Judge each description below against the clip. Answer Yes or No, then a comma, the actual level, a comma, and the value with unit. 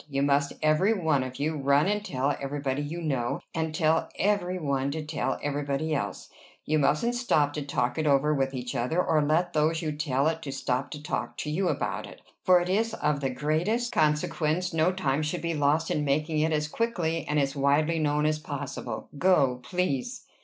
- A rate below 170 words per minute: No, fast, 205 wpm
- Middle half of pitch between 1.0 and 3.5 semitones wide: Yes, average, 2.7 semitones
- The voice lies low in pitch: No, medium, 150 Hz